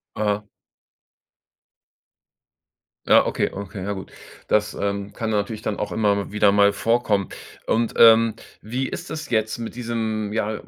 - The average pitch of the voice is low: Yes, low, 105 Hz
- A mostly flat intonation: Yes, narrow, 2.0 semitones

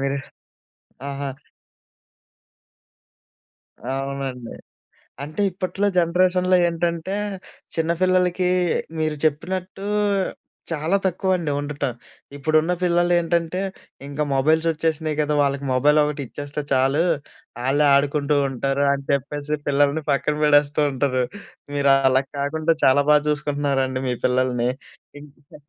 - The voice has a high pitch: No, medium, 150 Hz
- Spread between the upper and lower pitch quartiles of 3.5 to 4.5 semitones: No, average, 3.0 semitones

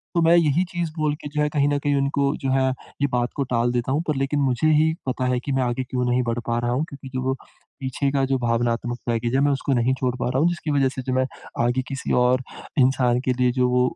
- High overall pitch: No, low, 130 Hz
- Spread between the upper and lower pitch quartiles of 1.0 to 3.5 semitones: Yes, narrow, 2.4 semitones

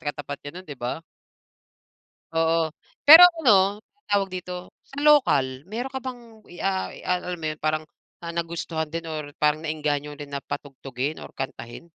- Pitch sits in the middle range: Yes, medium, 160 Hz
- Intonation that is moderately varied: Yes, average, 4.3 semitones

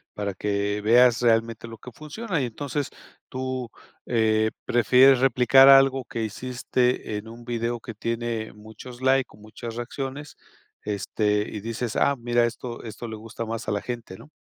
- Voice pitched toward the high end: No, low, 120 Hz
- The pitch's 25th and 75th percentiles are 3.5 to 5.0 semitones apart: No, narrow, 2.6 semitones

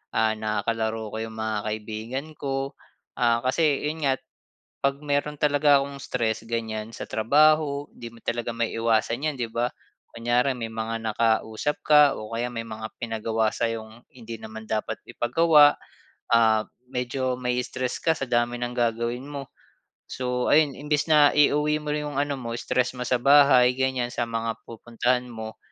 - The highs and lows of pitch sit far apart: No, average, 3.6 semitones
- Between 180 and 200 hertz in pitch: No, low, 120 Hz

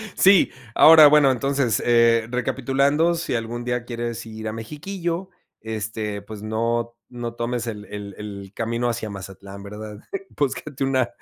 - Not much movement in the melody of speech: No, average, 3.8 semitones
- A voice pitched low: Yes, low, 120 Hz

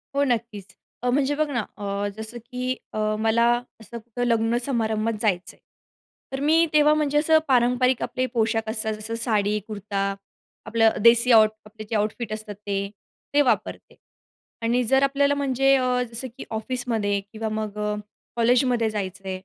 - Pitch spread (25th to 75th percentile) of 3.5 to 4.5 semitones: No, average, 2.9 semitones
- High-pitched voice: Yes, high, 230 Hz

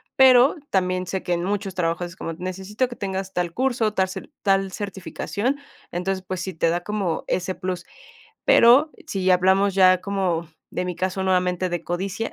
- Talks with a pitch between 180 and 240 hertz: Yes, high, 190 Hz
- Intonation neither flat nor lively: No, narrow, 1.8 semitones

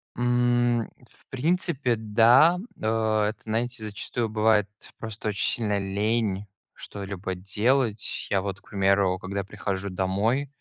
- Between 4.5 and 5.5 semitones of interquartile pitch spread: No, average, 3.3 semitones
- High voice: No, low, 110 Hz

